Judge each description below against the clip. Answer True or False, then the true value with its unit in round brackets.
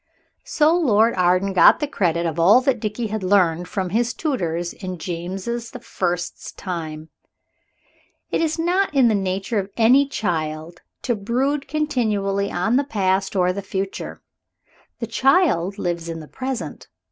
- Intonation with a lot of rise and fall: True (5.7 semitones)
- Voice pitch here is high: True (200 Hz)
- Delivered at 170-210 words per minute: False (155 wpm)